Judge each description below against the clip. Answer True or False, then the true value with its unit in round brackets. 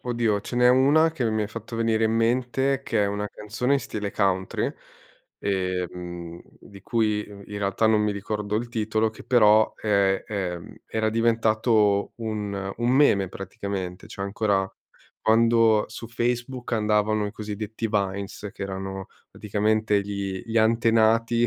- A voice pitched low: True (110 Hz)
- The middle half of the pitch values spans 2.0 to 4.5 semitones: True (2.5 semitones)